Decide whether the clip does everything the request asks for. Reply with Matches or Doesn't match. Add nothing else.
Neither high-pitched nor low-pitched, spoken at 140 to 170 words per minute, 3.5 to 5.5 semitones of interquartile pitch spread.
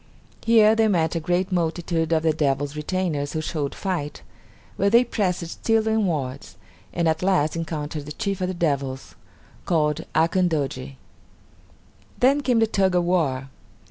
Matches